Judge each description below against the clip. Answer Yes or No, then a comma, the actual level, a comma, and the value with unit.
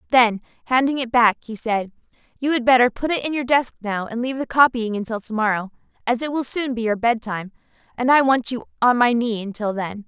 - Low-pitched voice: No, high, 240 Hz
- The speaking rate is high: Yes, fast, 225 wpm